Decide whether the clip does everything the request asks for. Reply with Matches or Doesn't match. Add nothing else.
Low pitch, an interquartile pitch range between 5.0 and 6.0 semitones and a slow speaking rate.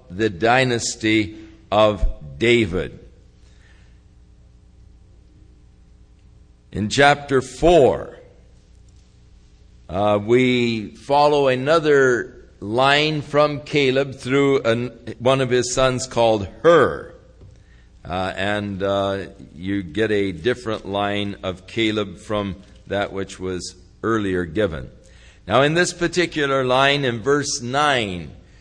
Matches